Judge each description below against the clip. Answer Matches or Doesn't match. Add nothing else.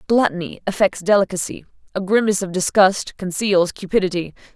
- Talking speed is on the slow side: Matches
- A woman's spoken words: Matches